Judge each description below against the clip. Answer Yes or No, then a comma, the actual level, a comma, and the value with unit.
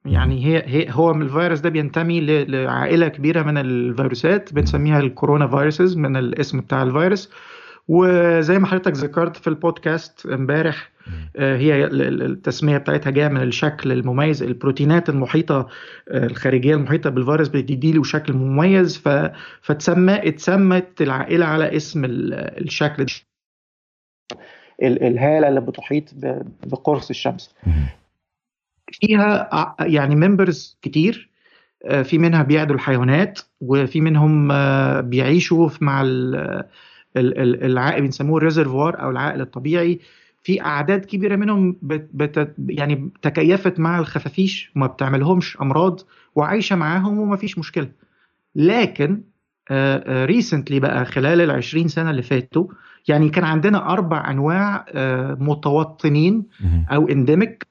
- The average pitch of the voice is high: No, medium, 155 Hz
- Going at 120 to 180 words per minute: No, average, 105 wpm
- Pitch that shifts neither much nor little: Yes, average, 4.0 semitones